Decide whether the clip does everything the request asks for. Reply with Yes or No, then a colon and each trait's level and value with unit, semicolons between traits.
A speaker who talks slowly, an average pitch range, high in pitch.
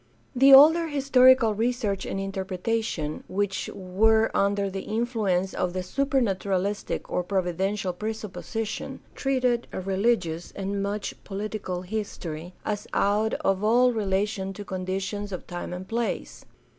Yes: slow, 125 wpm; average, 3.0 semitones; high, 200 Hz